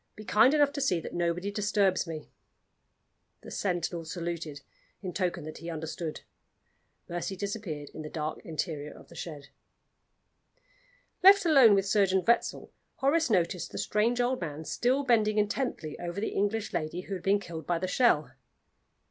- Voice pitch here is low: No, medium, 185 Hz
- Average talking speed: Yes, average, 160 wpm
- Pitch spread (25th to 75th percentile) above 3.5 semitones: Yes, average, 4.5 semitones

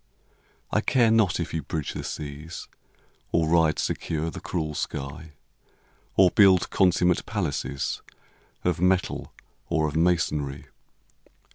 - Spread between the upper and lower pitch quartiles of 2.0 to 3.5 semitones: Yes, average, 2.9 semitones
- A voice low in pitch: Yes, very low, 85 Hz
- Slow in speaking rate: Yes, slow, 120 wpm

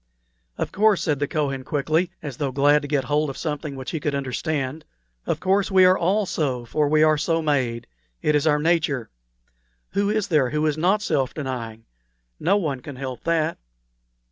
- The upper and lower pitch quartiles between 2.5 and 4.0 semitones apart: Yes, average, 3.4 semitones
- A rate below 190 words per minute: No, average, 195 wpm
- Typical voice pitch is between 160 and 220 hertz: No, medium, 150 Hz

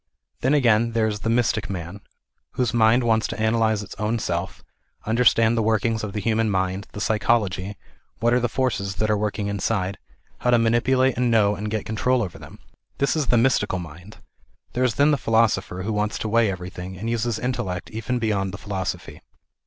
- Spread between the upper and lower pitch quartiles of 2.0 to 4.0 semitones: Yes, average, 2.7 semitones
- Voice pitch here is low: Yes, low, 110 Hz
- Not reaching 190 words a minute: No, average, 200 wpm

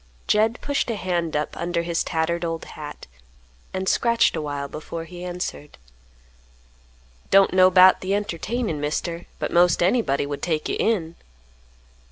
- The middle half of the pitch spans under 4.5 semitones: Yes, average, 2.8 semitones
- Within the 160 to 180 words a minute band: No, average, 145 wpm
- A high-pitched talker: No, medium, 175 Hz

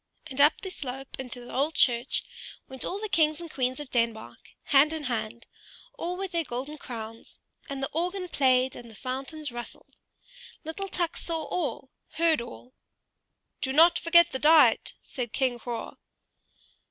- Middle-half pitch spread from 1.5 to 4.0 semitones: No, average, 4.7 semitones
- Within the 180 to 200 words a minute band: No, average, 165 wpm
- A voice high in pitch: Yes, very high, 275 Hz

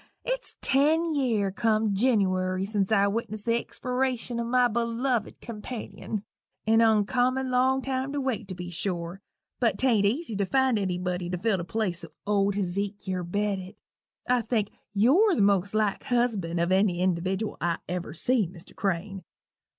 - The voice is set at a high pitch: Yes, high, 210 Hz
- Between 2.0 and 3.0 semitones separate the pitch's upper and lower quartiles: No, average, 4.6 semitones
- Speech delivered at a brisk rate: No, average, 155 wpm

